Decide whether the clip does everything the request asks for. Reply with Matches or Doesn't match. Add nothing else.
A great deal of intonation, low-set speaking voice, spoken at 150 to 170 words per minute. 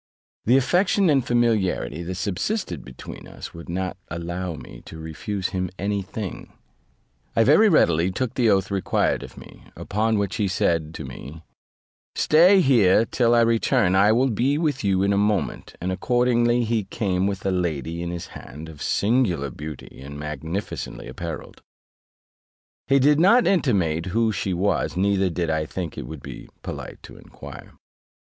Matches